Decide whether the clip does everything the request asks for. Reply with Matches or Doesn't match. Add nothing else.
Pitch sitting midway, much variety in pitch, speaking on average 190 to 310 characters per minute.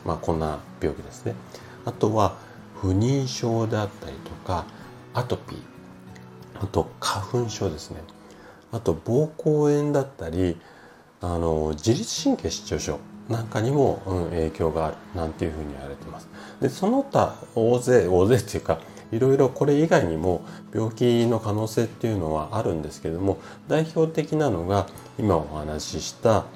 Doesn't match